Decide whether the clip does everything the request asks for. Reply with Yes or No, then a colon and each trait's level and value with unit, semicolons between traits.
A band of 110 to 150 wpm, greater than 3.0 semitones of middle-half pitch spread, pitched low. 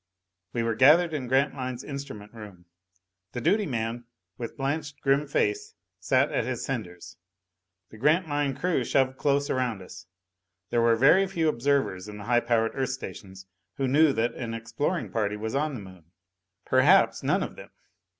No: average, 165 wpm; average, 4.2 semitones; low, 130 Hz